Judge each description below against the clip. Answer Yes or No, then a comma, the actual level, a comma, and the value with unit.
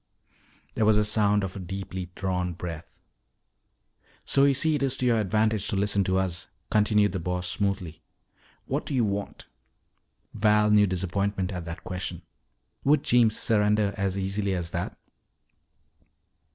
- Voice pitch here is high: No, low, 100 Hz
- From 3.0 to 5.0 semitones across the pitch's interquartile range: No, narrow, 2.5 semitones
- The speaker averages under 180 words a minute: Yes, average, 150 wpm